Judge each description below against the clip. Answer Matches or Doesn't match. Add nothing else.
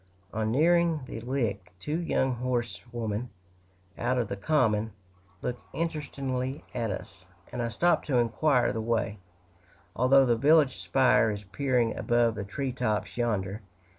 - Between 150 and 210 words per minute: Doesn't match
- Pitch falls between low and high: Doesn't match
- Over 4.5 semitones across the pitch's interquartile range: Doesn't match